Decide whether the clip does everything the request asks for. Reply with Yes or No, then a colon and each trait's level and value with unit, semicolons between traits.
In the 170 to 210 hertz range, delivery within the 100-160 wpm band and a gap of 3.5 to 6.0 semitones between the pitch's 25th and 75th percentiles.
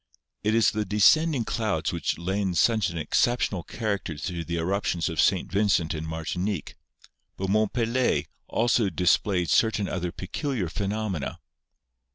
No: very low, 95 Hz; average, 150 wpm; average, 4.1 semitones